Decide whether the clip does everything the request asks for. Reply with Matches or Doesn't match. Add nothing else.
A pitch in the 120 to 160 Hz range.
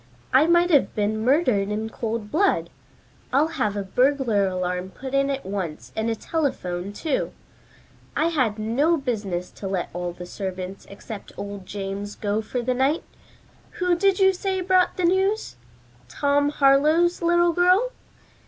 Doesn't match